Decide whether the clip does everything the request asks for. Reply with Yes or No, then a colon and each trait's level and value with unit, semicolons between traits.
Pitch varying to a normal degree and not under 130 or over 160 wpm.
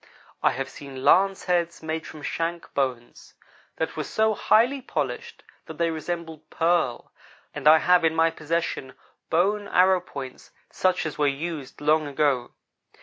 Yes: average, 3.6 semitones; average, 150 wpm